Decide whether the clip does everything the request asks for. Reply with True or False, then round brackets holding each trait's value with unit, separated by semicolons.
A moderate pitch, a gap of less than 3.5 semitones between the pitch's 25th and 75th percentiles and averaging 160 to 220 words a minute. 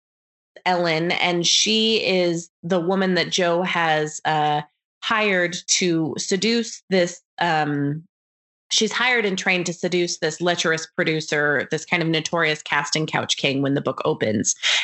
False (175 Hz; 2.9 semitones; 140 wpm)